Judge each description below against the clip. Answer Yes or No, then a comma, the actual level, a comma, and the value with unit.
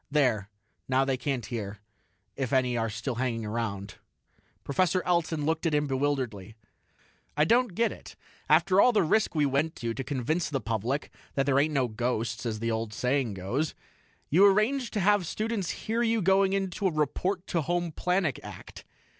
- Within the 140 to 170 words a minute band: No, average, 180 wpm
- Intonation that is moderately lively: No, wide, 7.4 semitones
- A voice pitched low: No, medium, 145 Hz